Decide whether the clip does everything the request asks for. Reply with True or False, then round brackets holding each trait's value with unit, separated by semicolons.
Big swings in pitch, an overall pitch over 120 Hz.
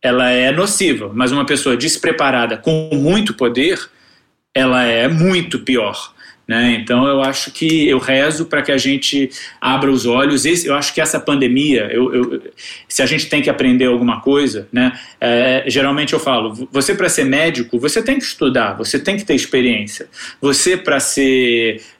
False (3.3 semitones; 135 Hz)